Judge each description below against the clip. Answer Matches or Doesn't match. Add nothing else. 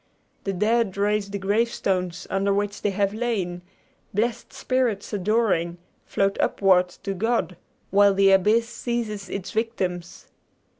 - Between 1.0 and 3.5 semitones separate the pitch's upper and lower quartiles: Matches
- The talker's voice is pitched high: Matches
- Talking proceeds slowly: Matches